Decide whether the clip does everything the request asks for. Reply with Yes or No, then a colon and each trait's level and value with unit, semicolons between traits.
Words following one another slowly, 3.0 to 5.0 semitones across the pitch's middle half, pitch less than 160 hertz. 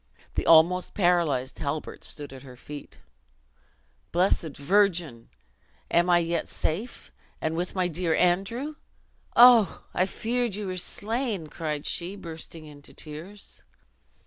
No: slow, 125 wpm; average, 4.1 semitones; medium, 175 Hz